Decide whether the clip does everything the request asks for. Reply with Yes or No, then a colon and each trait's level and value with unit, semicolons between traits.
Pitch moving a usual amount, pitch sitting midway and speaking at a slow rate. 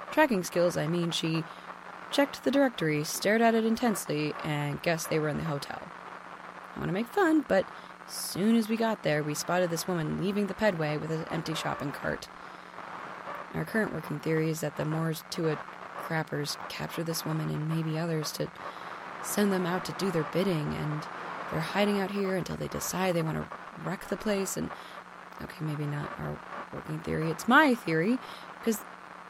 No: average, 4.2 semitones; medium, 170 Hz; average, 190 wpm